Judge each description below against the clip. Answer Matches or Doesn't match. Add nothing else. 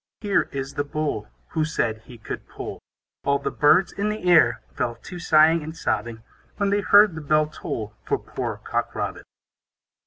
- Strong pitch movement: Matches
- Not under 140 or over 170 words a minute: Doesn't match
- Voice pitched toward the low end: Doesn't match